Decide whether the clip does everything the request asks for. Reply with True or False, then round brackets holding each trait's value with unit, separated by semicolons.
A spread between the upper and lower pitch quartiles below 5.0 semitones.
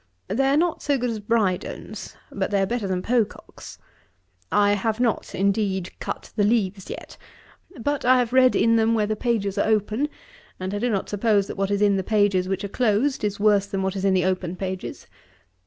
True (3.0 semitones)